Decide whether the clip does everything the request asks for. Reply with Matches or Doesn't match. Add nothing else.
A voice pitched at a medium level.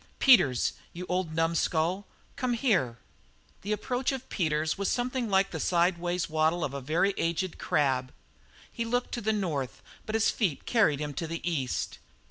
Matches